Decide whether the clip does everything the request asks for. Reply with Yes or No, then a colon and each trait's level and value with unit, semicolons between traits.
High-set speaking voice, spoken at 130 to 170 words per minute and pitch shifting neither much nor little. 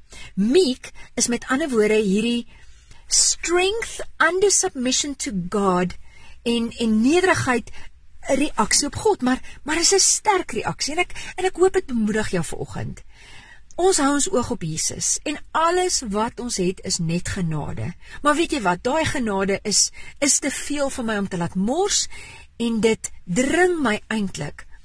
No: high, 245 Hz; average, 160 wpm; wide, 7.5 semitones